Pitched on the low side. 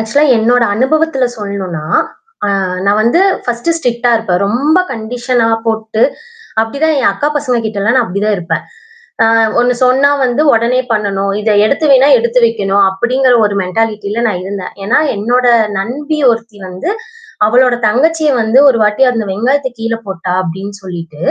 No: high, 230 Hz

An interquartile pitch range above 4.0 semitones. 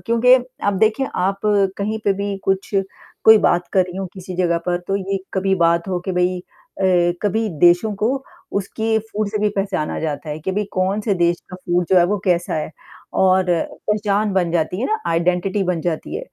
No: average, 2.8 semitones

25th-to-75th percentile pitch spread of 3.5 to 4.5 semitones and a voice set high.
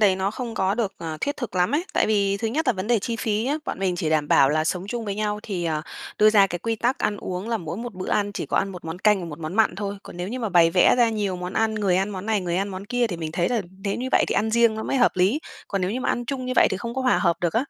Yes: average, 4.0 semitones; high, 205 Hz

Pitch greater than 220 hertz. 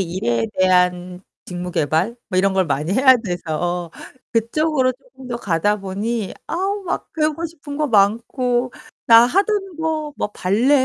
Yes: high, 230 Hz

